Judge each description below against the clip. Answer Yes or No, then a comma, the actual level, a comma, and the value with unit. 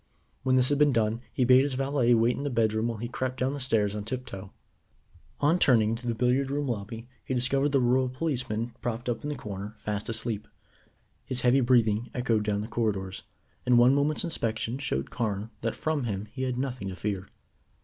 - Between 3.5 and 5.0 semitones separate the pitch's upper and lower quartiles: No, average, 3.0 semitones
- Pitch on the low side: Yes, low, 120 Hz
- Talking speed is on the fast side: Yes, fast, 210 wpm